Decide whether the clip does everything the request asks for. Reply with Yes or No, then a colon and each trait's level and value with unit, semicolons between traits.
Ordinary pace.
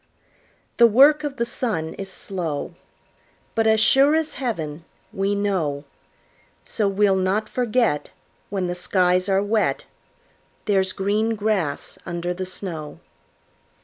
No: slow, 125 wpm